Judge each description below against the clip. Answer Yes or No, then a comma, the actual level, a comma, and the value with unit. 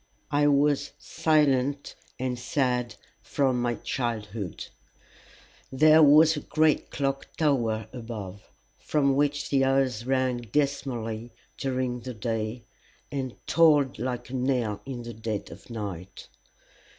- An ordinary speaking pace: No, slow, 120 wpm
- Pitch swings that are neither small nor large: Yes, average, 3.4 semitones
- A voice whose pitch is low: Yes, low, 130 Hz